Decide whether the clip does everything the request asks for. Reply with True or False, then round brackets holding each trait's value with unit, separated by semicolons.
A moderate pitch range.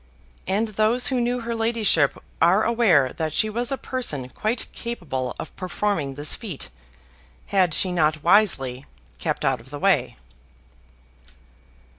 False (7.7 semitones)